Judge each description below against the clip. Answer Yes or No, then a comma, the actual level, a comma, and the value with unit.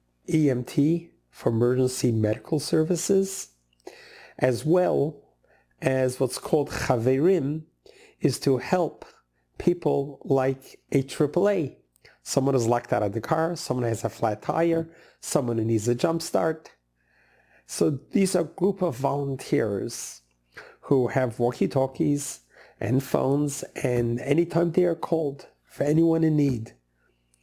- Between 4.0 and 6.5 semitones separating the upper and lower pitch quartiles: Yes, wide, 5.4 semitones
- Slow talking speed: Yes, slow, 125 wpm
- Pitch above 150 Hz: No, low, 135 Hz